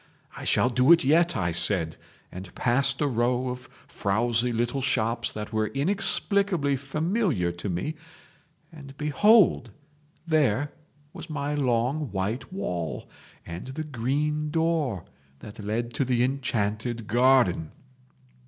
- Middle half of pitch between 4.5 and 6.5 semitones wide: Yes, wide, 5.5 semitones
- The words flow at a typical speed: No, slow, 125 wpm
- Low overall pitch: Yes, low, 125 Hz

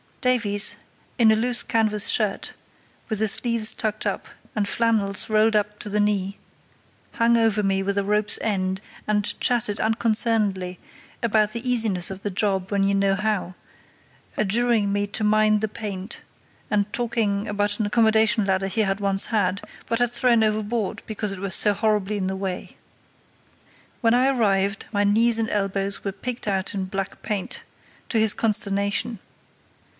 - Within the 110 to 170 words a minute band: Yes, average, 165 wpm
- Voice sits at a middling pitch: No, high, 210 Hz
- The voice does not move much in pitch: Yes, narrow, 2.1 semitones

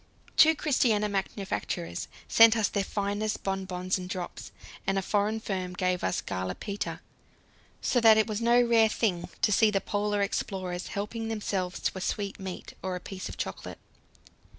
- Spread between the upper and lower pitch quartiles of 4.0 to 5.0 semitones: No, average, 2.9 semitones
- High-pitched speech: Yes, high, 200 Hz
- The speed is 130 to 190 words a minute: Yes, average, 165 wpm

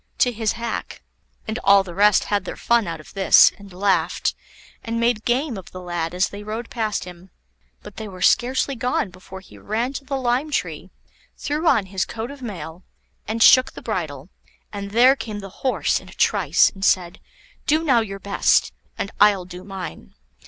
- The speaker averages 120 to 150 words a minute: No, average, 195 wpm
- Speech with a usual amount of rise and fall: Yes, average, 4.4 semitones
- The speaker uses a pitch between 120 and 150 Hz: No, high, 205 Hz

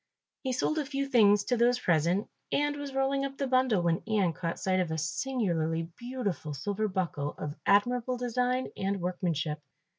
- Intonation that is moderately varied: No, wide, 7.0 semitones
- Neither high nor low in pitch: No, high, 205 Hz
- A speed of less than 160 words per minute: No, average, 175 wpm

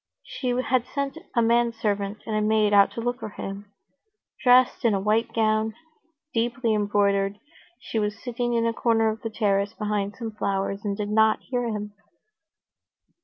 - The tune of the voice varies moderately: No, narrow, 2.3 semitones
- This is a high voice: Yes, high, 220 Hz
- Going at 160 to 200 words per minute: Yes, average, 170 wpm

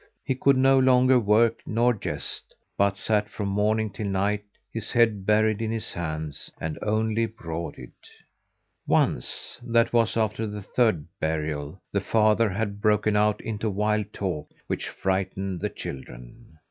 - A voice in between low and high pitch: No, low, 105 Hz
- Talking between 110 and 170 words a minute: Yes, average, 145 wpm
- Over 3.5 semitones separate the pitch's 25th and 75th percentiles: No, average, 2.8 semitones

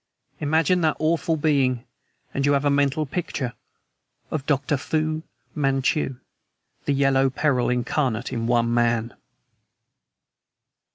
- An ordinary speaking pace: No, slow, 115 wpm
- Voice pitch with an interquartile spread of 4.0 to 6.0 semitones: No, average, 3.6 semitones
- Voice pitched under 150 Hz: Yes, medium, 140 Hz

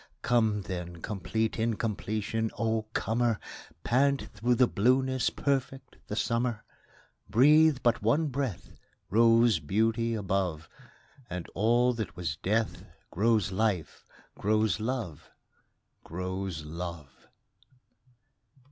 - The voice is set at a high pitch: No, low, 110 Hz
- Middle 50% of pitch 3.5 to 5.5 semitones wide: Yes, average, 4.1 semitones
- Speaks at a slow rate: Yes, slow, 100 wpm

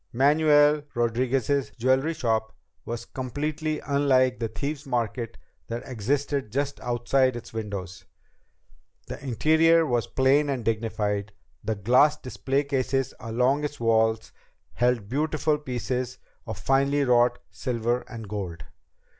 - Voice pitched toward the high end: No, low, 125 Hz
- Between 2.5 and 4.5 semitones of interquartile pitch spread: Yes, average, 3.7 semitones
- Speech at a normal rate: No, slow, 120 wpm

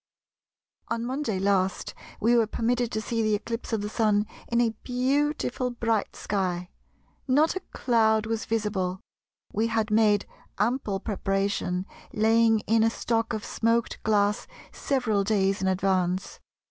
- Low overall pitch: No, high, 220 Hz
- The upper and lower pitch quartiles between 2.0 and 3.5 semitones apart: Yes, narrow, 2.5 semitones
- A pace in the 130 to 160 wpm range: Yes, average, 145 wpm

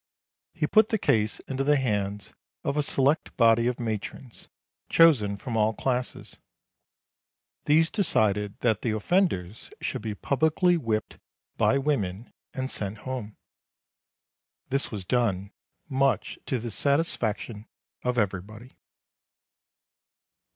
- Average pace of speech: No, slow, 115 wpm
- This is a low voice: Yes, low, 120 Hz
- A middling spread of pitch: Yes, average, 4.6 semitones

